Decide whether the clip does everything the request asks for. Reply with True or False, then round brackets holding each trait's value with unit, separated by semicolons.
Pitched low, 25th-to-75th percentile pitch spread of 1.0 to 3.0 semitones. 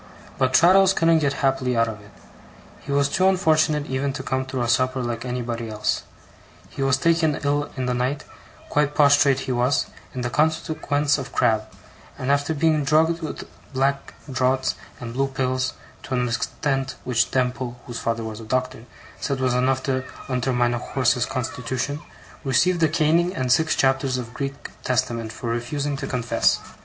True (130 Hz; 2.7 semitones)